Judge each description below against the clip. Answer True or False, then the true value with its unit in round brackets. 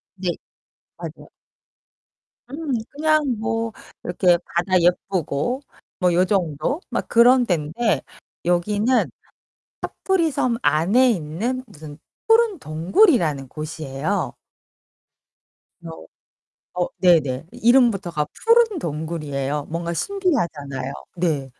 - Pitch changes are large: True (8.4 semitones)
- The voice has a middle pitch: True (180 Hz)